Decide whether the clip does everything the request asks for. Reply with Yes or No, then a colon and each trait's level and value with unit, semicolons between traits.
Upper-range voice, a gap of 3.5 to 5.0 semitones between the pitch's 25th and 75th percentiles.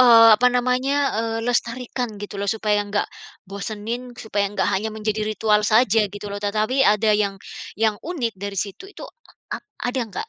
No: high, 220 Hz; average, 2.9 semitones